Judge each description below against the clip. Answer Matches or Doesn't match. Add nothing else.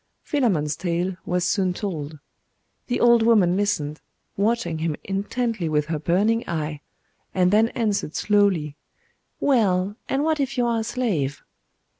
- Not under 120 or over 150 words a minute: Matches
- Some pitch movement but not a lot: Doesn't match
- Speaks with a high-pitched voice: Matches